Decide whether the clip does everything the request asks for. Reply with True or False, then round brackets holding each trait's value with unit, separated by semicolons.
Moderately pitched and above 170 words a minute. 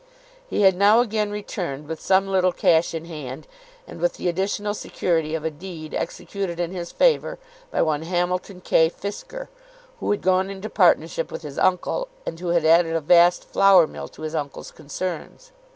True (175 Hz; 185 wpm)